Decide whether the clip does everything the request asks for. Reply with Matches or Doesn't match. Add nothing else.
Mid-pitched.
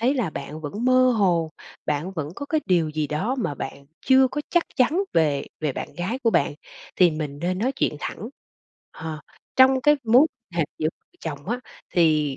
Matches